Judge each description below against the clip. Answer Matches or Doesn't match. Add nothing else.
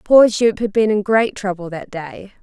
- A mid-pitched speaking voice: Doesn't match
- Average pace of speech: Doesn't match